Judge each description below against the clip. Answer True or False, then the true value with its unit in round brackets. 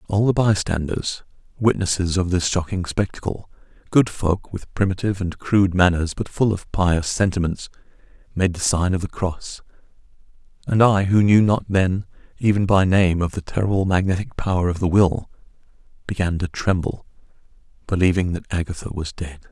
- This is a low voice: True (95 Hz)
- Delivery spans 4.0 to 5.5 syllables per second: True (5.2 syllables/s)